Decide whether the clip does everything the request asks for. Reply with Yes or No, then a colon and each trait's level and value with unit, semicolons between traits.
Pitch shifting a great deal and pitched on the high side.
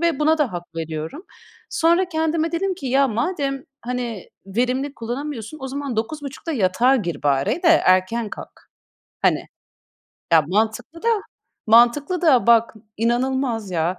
Yes: wide, 5.8 semitones; very high, 250 Hz